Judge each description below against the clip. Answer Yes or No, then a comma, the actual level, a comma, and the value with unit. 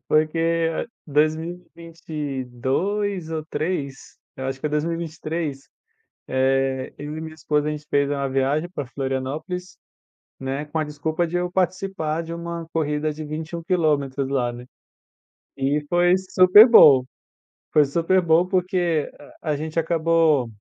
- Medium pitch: Yes, medium, 155 Hz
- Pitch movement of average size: Yes, average, 3.0 semitones